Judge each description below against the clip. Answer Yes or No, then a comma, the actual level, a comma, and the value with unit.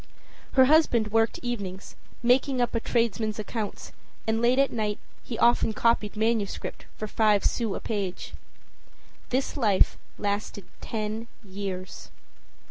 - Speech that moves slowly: Yes, slow, 130 wpm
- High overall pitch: Yes, high, 220 Hz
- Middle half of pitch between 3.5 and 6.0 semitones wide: No, narrow, 2.6 semitones